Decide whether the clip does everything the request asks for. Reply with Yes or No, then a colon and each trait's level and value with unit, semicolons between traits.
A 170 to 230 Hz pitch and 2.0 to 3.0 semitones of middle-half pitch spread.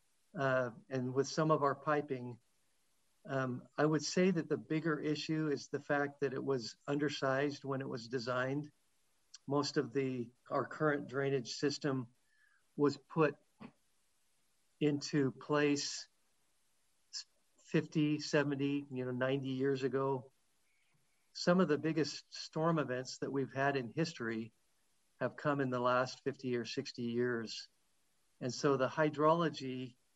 No: medium, 140 Hz; narrow, 2.5 semitones